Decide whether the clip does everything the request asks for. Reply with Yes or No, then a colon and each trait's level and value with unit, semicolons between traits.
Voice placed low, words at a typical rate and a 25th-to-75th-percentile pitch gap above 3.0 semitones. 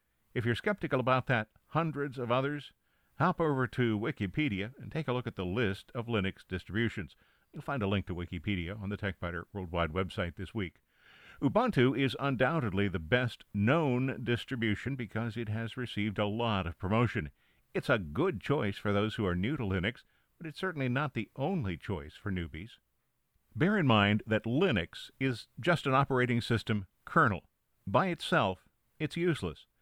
Yes: low, 115 Hz; average, 170 wpm; average, 4.5 semitones